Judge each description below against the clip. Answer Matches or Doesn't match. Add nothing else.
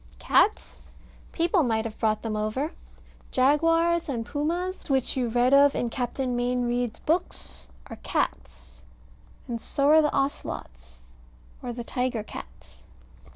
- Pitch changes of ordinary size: Matches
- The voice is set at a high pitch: Matches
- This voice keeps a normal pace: Doesn't match